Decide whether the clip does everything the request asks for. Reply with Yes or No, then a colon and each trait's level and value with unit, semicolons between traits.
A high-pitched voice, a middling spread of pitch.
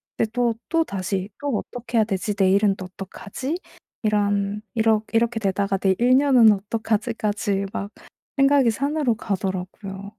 Yes: high, 210 Hz; average, 3.1 semitones